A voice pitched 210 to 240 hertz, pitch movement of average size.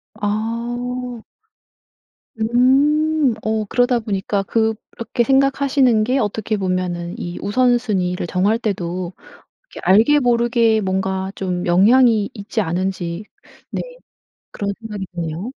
Yes: high, 220 Hz; average, 4.3 semitones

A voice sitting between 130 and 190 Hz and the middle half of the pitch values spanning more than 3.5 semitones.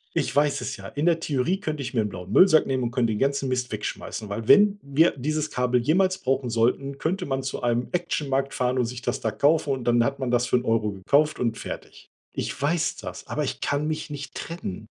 Yes: low, 135 Hz; average, 4.1 semitones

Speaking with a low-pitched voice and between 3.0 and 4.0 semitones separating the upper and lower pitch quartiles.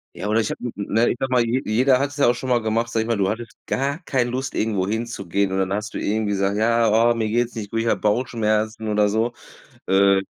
No: low, 110 Hz; narrow, 2.4 semitones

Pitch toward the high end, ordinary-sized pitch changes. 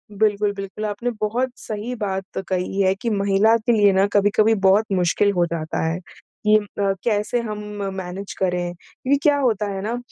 No: high, 205 Hz; narrow, 2.2 semitones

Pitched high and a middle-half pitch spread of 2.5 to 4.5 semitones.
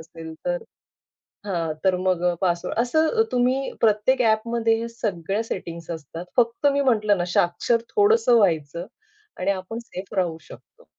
No: high, 205 Hz; average, 5.3 semitones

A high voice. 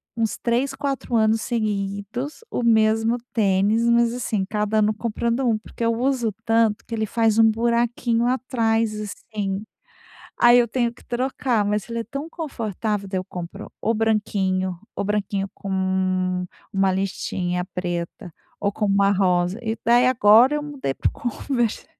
Yes: high, 220 Hz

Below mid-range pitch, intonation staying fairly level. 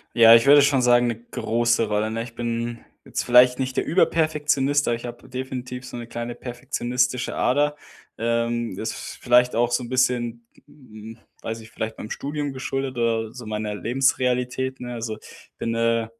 Yes: low, 120 Hz; narrow, 1.9 semitones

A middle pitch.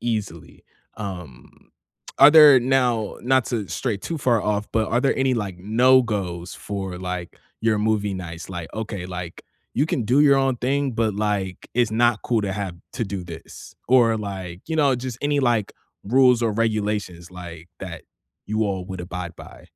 No: low, 110 Hz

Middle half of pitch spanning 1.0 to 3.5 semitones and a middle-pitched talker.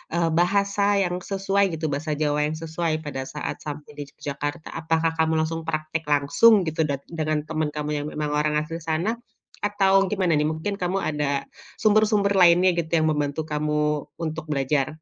Yes: average, 3.0 semitones; medium, 160 Hz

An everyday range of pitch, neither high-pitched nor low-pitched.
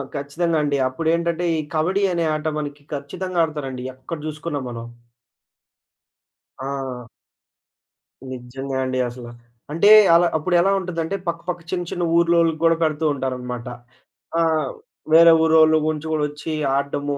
Yes: average, 3.3 semitones; medium, 155 Hz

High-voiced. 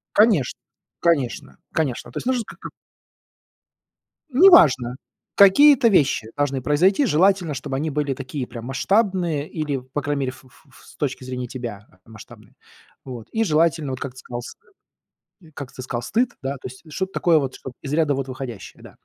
No: medium, 140 Hz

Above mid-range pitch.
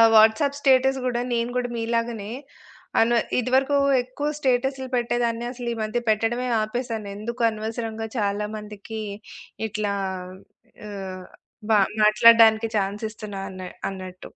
Yes: high, 225 Hz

